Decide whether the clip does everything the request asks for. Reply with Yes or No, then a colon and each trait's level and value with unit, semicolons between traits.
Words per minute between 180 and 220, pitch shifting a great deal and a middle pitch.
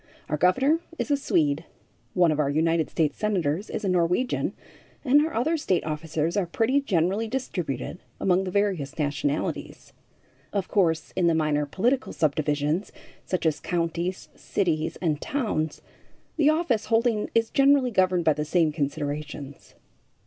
No: average, 150 wpm; wide, 6.3 semitones; medium, 175 Hz